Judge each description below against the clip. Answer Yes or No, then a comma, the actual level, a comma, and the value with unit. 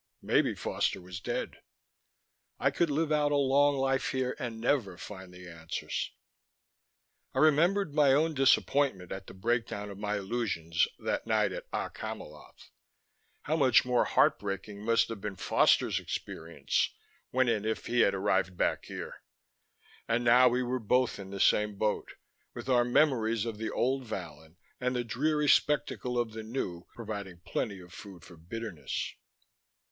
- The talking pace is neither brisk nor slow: Yes, average, 160 wpm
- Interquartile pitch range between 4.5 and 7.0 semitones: Yes, average, 5.1 semitones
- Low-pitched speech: Yes, low, 115 Hz